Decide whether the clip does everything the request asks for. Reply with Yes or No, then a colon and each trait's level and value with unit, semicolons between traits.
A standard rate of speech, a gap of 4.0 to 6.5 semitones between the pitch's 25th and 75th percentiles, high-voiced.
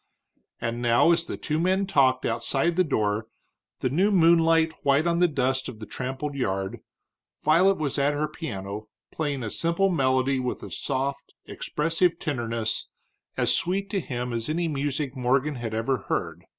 No: average, 165 wpm; average, 5.0 semitones; medium, 140 Hz